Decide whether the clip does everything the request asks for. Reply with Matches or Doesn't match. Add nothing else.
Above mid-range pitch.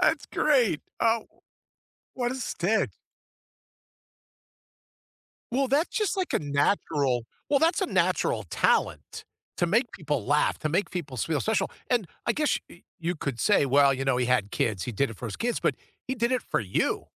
Doesn't match